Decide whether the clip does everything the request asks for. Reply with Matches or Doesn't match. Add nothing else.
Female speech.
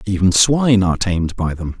Doesn't match